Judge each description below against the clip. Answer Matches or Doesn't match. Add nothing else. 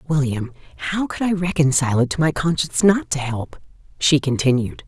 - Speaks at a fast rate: Doesn't match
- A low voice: Doesn't match